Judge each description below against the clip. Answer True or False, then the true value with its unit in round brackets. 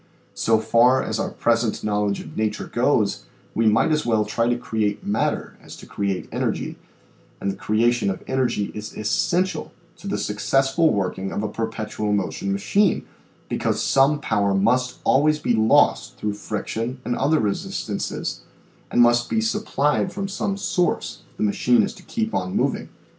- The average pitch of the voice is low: True (115 Hz)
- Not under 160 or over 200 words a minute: True (170 wpm)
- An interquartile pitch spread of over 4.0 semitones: True (4.6 semitones)